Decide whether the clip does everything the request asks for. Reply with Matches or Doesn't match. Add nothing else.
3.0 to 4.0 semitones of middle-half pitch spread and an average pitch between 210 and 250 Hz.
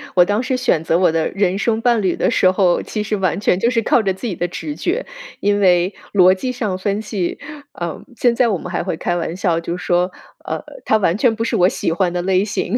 Doesn't match